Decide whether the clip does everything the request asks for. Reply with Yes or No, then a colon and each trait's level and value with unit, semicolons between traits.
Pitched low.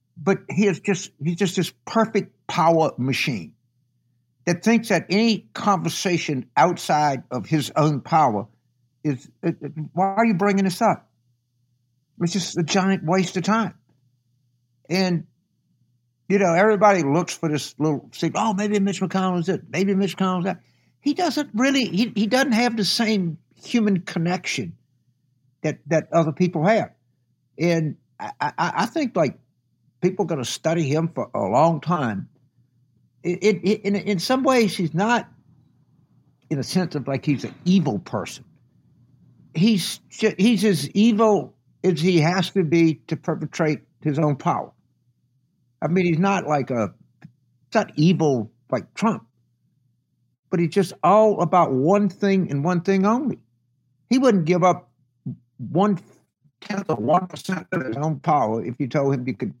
No: medium, 170 Hz